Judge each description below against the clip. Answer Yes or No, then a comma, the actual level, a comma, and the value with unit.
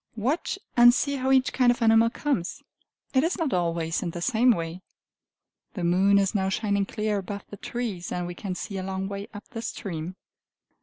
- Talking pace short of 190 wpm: No, average, 200 wpm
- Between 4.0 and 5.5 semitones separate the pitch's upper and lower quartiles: Yes, average, 4.9 semitones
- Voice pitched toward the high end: Yes, high, 200 Hz